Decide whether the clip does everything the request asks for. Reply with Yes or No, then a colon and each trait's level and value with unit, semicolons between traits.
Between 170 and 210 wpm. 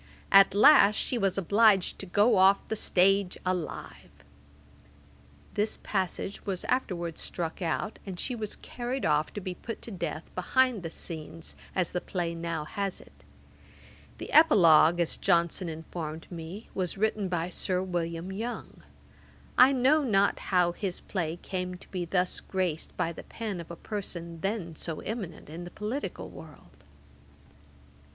No: average, 155 wpm